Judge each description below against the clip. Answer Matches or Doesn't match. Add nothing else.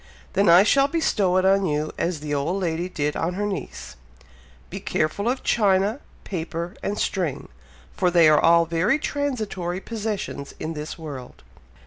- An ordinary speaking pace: Matches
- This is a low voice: Doesn't match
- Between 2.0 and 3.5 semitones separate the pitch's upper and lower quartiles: Doesn't match